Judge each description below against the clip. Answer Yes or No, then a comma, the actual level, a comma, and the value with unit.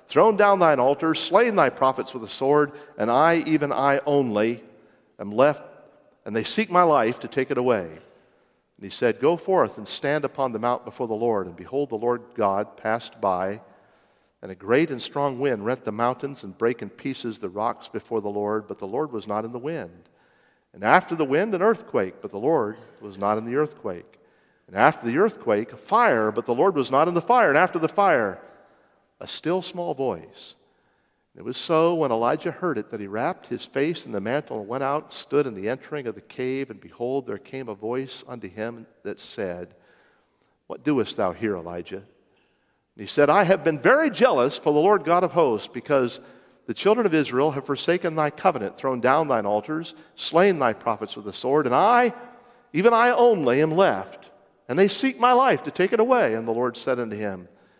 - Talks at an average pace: No, fast, 210 wpm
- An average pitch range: No, wide, 7.3 semitones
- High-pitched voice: No, medium, 140 Hz